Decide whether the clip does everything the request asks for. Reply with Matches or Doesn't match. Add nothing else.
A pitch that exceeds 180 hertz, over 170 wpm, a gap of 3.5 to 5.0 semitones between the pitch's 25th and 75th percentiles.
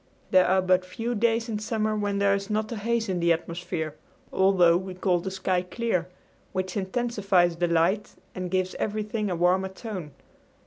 Doesn't match